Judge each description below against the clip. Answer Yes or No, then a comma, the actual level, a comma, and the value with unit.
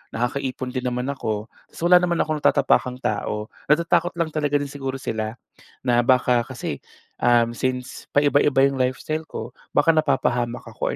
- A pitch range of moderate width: Yes, average, 3.4 semitones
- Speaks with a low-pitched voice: Yes, low, 130 Hz